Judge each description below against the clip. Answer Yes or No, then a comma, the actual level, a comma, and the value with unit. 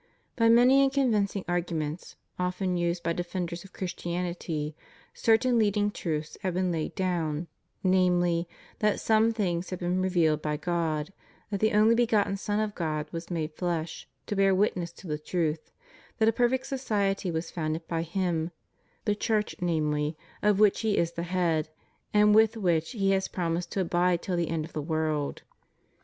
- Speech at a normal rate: Yes, average, 175 wpm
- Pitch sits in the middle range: Yes, medium, 180 Hz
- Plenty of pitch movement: No, average, 3.8 semitones